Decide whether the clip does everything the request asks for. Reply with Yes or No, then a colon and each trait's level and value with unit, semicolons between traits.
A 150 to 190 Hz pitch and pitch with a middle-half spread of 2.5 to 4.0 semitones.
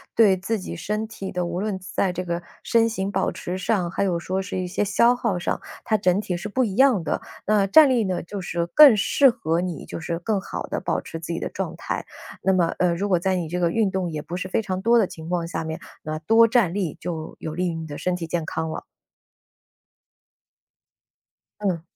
Yes: medium, 185 Hz; average, 3.6 semitones